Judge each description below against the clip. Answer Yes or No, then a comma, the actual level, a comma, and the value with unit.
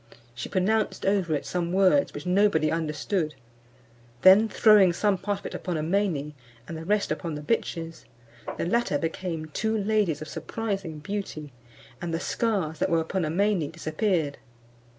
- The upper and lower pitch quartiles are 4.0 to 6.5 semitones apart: Yes, average, 4.3 semitones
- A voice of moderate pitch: Yes, medium, 180 Hz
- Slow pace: No, average, 155 wpm